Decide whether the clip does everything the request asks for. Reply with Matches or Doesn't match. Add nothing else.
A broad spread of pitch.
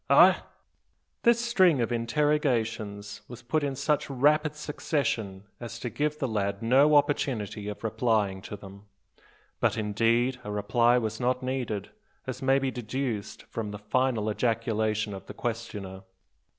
Doesn't match